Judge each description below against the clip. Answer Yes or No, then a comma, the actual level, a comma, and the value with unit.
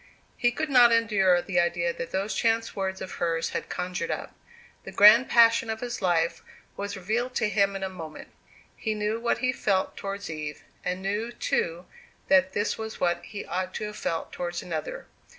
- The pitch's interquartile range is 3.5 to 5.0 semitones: Yes, average, 4.0 semitones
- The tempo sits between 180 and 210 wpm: Yes, average, 190 wpm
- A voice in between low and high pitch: No, high, 195 Hz